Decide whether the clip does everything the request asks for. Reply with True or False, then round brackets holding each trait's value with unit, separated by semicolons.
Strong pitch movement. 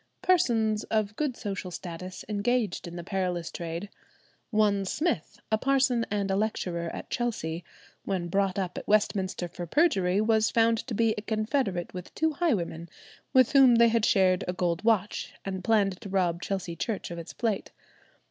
False (4.0 semitones)